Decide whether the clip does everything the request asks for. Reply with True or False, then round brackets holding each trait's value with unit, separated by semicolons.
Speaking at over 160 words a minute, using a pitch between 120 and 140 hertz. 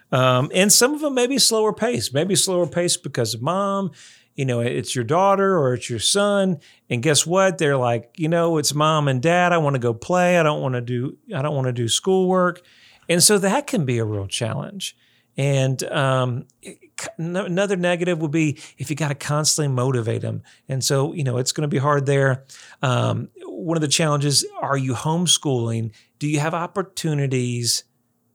False (200 wpm; 150 Hz)